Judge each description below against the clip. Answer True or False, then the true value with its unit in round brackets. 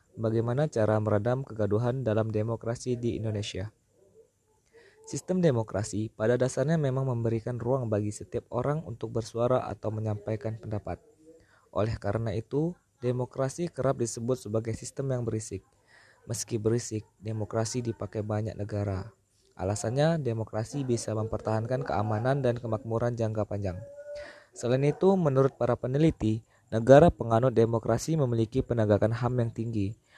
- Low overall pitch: True (115 Hz)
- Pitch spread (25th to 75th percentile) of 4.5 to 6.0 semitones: False (2.9 semitones)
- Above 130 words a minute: False (120 wpm)